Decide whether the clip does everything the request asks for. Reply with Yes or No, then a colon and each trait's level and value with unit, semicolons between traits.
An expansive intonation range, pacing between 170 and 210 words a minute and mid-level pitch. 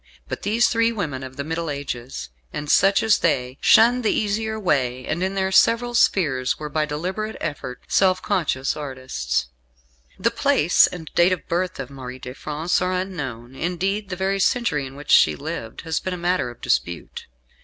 Yes: wide, 6.4 semitones; average, 185 wpm; medium, 165 Hz